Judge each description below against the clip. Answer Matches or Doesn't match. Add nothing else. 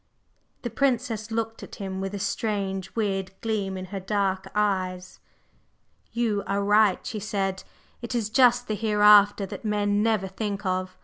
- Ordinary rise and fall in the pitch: Doesn't match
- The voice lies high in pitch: Matches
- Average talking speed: Matches